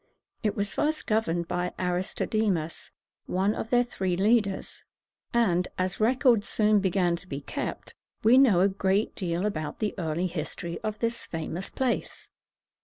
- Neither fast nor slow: Yes, average, 165 wpm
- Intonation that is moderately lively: Yes, average, 3.7 semitones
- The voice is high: Yes, high, 195 Hz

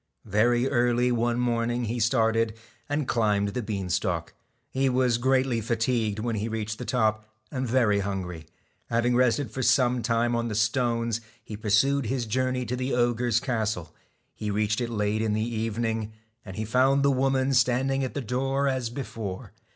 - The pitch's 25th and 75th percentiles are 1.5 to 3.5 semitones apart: Yes, average, 2.7 semitones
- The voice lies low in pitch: Yes, low, 120 Hz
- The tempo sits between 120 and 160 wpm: No, average, 175 wpm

